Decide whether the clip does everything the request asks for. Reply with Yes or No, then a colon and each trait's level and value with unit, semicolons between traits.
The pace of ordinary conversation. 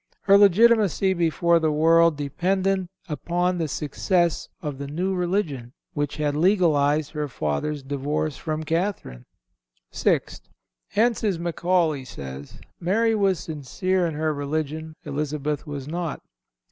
No: slow, 120 wpm